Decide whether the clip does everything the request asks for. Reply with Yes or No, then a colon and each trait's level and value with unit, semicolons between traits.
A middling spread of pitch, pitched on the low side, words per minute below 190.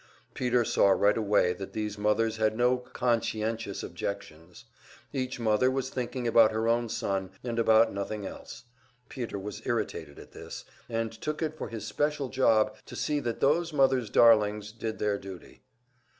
Yes: average, 3.0 semitones; low, 115 Hz; average, 165 wpm